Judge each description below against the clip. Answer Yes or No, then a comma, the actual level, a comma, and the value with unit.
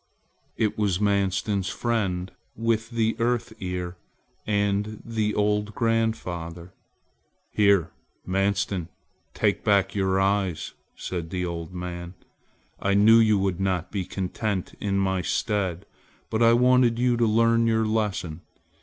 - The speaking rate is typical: No, slow, 130 wpm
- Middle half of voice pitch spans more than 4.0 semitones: No, average, 3.3 semitones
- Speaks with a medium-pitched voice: No, low, 100 Hz